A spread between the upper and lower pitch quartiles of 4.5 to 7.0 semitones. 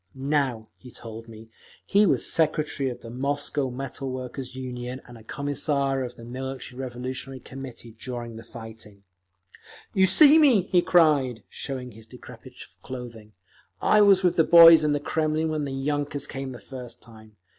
No: average, 3.4 semitones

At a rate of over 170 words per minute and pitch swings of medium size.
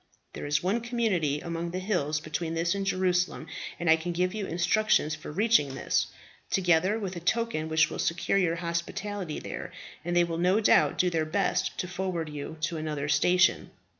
Yes: average, 190 wpm; average, 3.0 semitones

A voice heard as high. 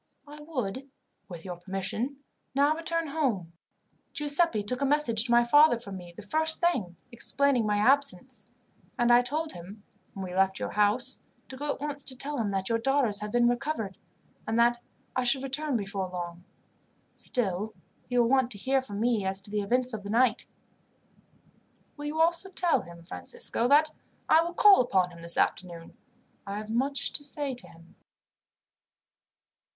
Yes: high, 240 Hz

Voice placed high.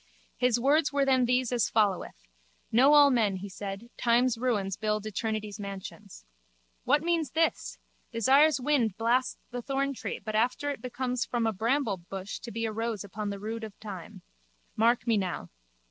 Yes: high, 230 Hz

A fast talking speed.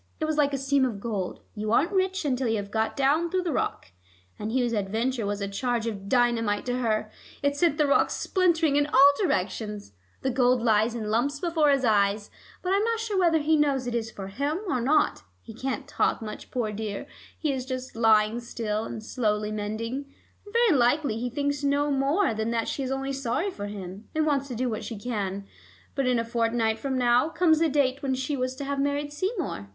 Yes: fast, 220 wpm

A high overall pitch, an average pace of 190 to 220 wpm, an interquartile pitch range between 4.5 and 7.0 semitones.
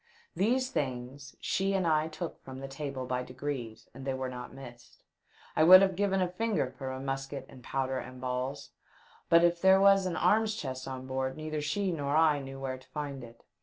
No: medium, 140 Hz; fast, 205 wpm; average, 4.8 semitones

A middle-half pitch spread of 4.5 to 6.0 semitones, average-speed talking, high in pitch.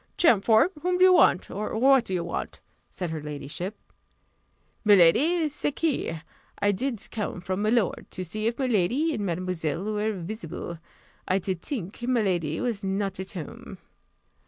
Yes: average, 5.2 semitones; average, 155 wpm; high, 205 Hz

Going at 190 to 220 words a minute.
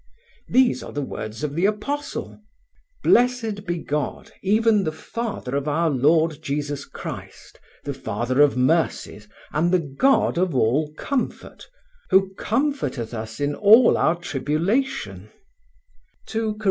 No: slow, 135 wpm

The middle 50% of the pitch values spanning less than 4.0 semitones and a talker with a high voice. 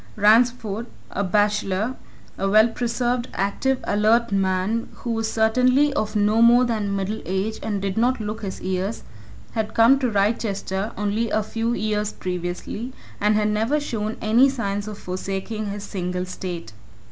Yes: narrow, 2.6 semitones; high, 215 Hz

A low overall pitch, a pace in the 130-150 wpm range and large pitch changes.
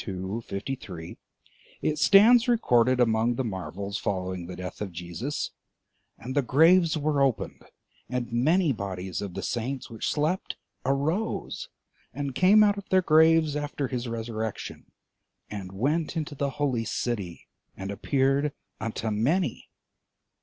Yes: low, 130 Hz; slow, 135 wpm; wide, 6.6 semitones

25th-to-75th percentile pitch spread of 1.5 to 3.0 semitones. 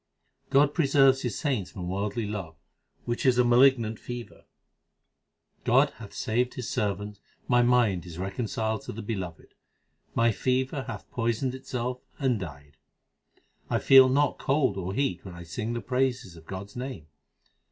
No: average, 4.7 semitones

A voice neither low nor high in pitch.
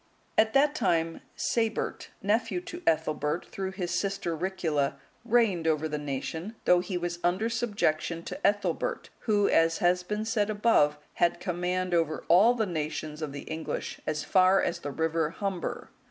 Yes: medium, 180 Hz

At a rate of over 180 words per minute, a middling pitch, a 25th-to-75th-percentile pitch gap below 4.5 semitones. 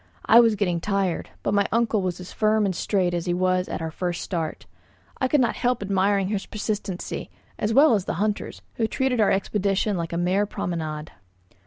No: average, 200 wpm; high, 195 Hz; average, 3.1 semitones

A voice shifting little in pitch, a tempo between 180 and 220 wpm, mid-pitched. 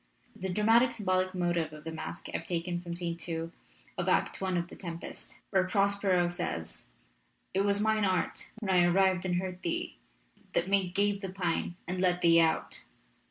Yes: narrow, 2.1 semitones; average, 185 wpm; medium, 180 Hz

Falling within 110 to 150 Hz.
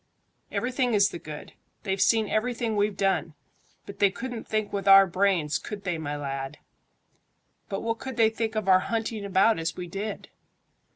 No: high, 200 Hz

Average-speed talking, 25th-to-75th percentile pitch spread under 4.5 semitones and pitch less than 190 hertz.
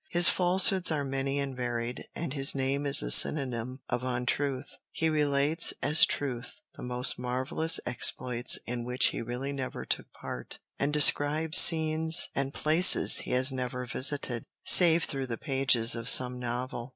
Yes: average, 160 wpm; average, 3.3 semitones; low, 135 Hz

